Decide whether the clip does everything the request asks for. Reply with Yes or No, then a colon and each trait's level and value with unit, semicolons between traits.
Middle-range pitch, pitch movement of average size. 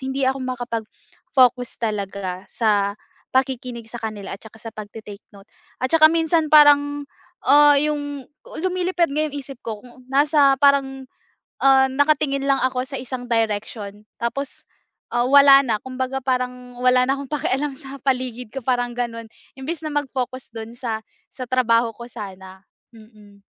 No: very high, 255 Hz; average, 3.4 semitones